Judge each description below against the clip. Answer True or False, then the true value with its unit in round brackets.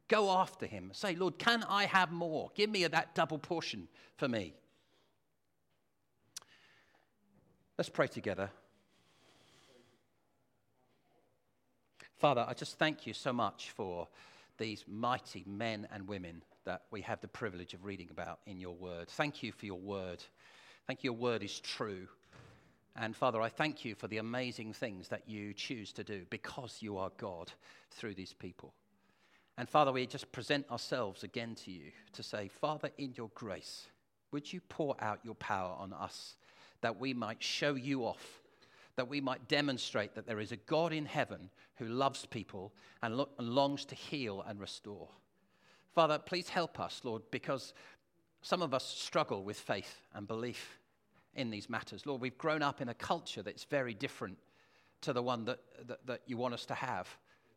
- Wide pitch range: True (5.8 semitones)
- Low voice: True (125 Hz)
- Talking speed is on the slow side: False (170 wpm)